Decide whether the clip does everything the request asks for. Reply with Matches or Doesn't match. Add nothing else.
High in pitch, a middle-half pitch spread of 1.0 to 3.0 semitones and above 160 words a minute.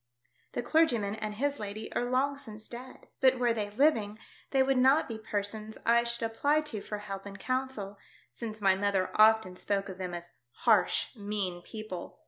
Doesn't match